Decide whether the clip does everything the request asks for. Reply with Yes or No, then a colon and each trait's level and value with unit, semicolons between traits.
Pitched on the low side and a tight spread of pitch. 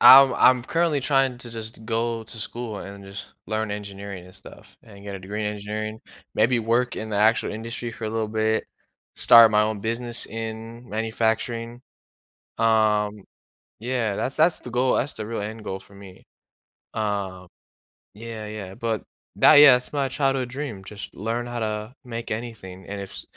Yes: low, 110 Hz; narrow, 2.2 semitones